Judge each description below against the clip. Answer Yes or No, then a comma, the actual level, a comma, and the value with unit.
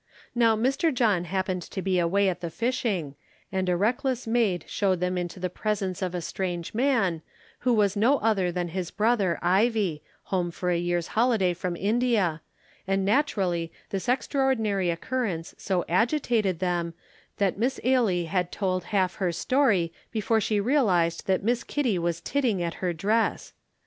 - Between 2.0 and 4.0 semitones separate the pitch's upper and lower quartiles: No, average, 4.5 semitones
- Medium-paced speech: Yes, average, 165 wpm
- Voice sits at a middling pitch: No, high, 195 Hz